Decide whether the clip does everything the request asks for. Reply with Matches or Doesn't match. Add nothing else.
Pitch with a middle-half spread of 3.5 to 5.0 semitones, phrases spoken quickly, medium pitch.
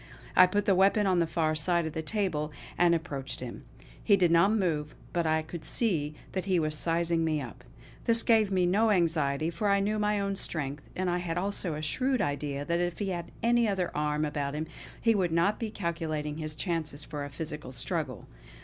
Matches